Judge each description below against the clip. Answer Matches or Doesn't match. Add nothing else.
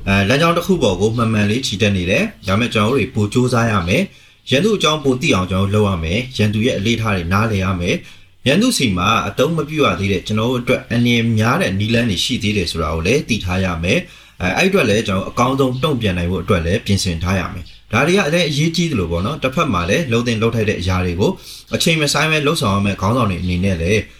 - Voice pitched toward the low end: Matches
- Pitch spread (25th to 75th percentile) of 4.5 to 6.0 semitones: Matches